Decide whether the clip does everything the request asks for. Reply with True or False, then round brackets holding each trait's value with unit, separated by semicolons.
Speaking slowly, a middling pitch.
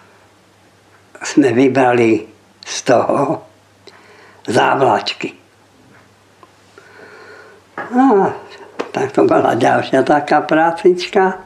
True (70 wpm; 180 Hz)